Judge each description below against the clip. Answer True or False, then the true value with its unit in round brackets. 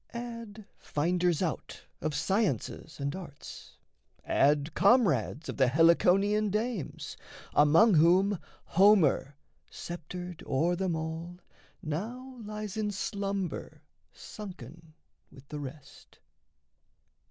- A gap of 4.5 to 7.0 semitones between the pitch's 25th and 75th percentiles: True (5.0 semitones)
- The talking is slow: True (95 wpm)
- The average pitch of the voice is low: False (175 Hz)